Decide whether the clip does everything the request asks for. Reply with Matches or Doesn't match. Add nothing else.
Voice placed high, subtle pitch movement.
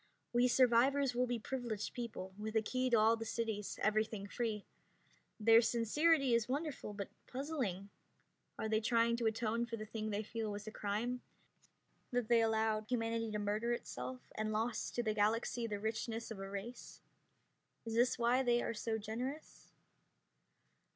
Matches